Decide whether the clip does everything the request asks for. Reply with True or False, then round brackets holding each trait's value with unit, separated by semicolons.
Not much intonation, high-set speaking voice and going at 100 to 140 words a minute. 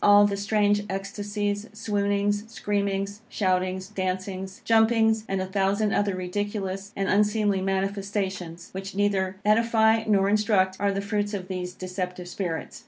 True (1.5 semitones; 200 Hz; 135 wpm)